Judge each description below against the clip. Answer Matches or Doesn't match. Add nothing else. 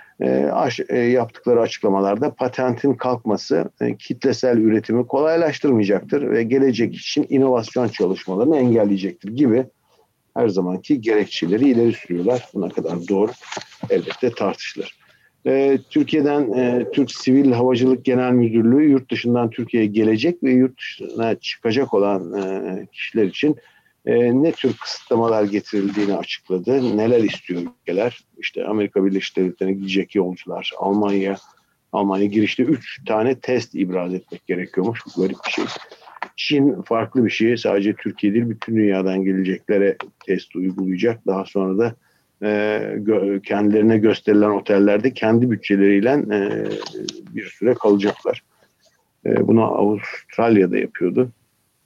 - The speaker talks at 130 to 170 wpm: Doesn't match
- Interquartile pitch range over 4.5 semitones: Doesn't match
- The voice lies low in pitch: Matches